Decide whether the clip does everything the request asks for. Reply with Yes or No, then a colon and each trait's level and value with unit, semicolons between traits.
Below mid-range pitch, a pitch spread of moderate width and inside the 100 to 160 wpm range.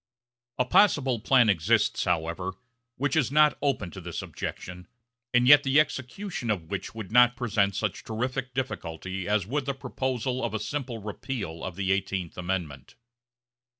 No: low, 110 Hz; wide, 5.8 semitones; average, 155 wpm